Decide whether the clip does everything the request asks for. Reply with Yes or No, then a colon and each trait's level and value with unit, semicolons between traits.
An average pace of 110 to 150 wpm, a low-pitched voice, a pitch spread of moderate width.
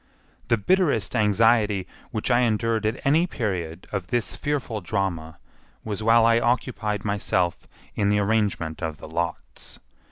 Yes: average, 140 wpm; low, 105 Hz; average, 3.6 semitones